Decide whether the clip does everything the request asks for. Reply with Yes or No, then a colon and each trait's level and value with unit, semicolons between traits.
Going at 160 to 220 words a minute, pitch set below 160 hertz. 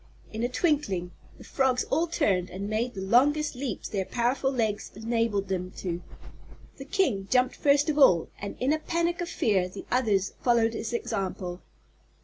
No: average, 170 wpm; high, 235 Hz